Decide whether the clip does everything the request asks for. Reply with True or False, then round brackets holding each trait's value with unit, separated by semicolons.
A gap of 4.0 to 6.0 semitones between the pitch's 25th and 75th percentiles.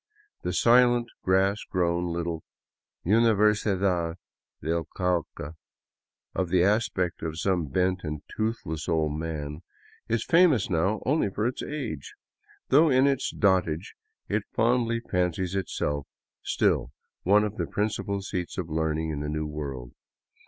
True (5.1 semitones)